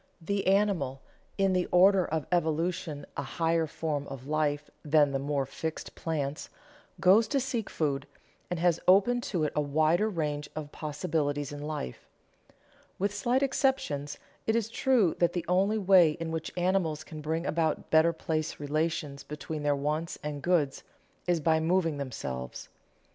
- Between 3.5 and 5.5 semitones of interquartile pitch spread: Yes, average, 3.8 semitones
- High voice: No, medium, 160 Hz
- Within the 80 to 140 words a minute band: No, average, 160 wpm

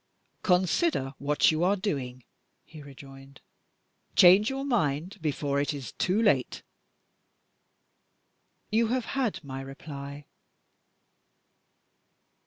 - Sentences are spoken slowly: Yes, slow, 95 wpm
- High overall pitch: No, medium, 150 Hz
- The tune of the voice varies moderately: No, wide, 6.8 semitones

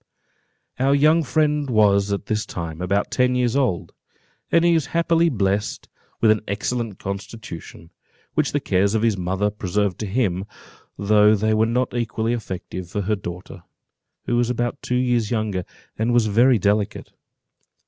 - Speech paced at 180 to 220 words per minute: No, average, 160 wpm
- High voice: No, low, 110 Hz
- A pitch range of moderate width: Yes, average, 3.9 semitones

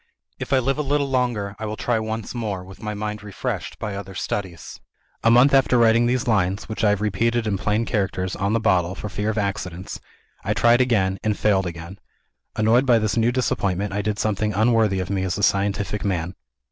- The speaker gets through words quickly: Yes, fast, 210 wpm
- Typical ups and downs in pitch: Yes, average, 3.0 semitones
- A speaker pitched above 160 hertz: No, low, 105 Hz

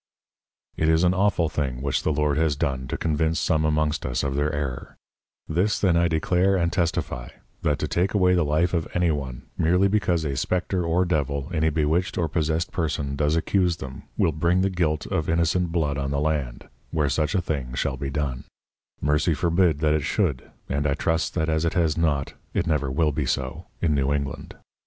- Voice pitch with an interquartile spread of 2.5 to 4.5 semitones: Yes, average, 3.0 semitones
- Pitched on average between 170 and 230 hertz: No, very low, 80 Hz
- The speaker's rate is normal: No, fast, 210 wpm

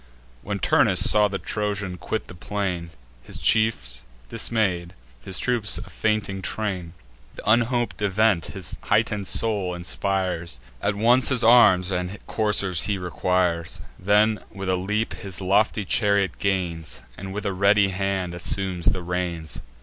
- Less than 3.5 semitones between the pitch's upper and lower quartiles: Yes, average, 2.7 semitones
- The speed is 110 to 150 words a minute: Yes, average, 140 wpm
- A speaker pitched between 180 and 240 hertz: No, very low, 95 Hz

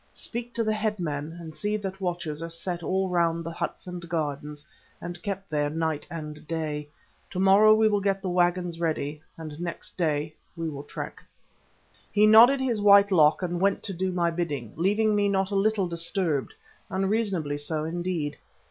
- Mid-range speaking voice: Yes, medium, 175 Hz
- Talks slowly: No, average, 175 wpm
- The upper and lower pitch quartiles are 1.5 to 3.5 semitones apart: No, average, 4.0 semitones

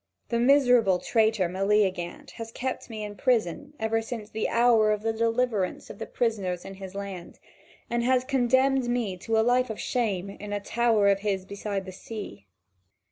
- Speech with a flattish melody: No, average, 3.4 semitones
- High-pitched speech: Yes, high, 220 Hz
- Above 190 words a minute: No, average, 180 wpm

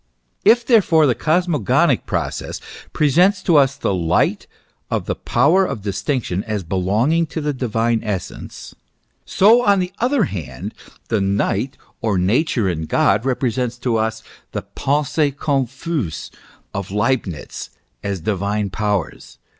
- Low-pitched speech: Yes, low, 120 Hz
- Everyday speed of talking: No, slow, 130 wpm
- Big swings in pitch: Yes, wide, 7.4 semitones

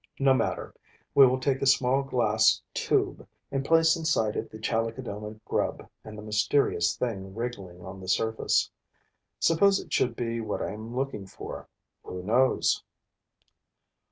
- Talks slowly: No, average, 150 wpm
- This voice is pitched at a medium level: No, low, 115 Hz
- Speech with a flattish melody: No, average, 4.0 semitones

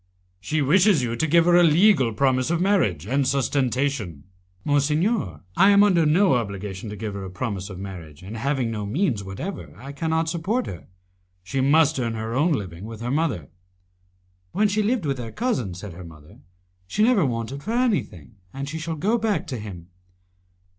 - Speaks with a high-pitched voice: No, low, 135 Hz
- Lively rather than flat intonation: Yes, wide, 8.5 semitones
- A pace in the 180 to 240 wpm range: Yes, average, 185 wpm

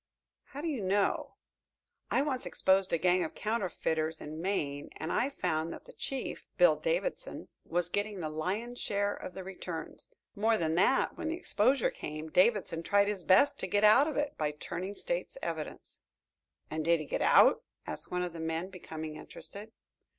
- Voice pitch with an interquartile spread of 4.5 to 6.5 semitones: Yes, wide, 5.6 semitones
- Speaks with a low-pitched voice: No, high, 190 Hz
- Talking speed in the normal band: Yes, average, 180 wpm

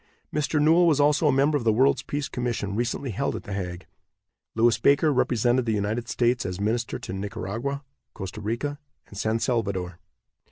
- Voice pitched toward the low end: Yes, low, 120 Hz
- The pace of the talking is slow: No, average, 175 wpm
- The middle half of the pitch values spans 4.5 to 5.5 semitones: Yes, average, 5.2 semitones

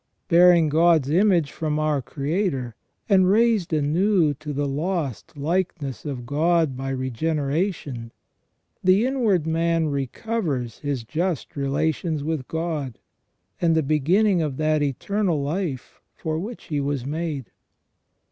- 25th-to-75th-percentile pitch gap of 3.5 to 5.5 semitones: Yes, average, 3.9 semitones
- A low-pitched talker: No, medium, 155 Hz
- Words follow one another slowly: Yes, slow, 125 wpm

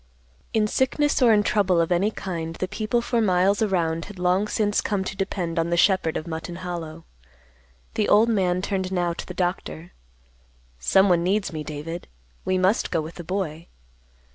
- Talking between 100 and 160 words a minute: No, average, 180 wpm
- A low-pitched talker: No, medium, 185 Hz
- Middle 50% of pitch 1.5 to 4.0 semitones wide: Yes, average, 3.3 semitones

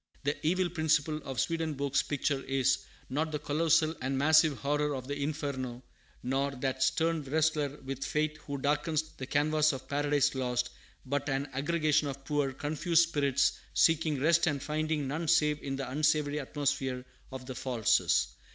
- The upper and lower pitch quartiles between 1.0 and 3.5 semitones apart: Yes, narrow, 2.4 semitones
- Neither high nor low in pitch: Yes, medium, 145 Hz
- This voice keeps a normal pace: Yes, average, 160 wpm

